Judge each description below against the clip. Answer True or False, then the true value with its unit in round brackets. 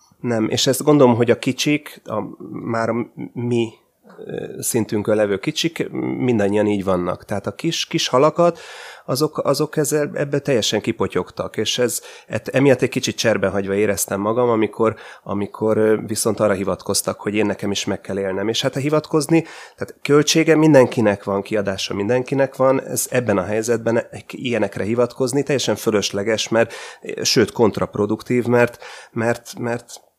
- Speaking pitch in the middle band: False (115 Hz)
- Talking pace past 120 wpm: True (145 wpm)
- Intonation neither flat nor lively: True (4.2 semitones)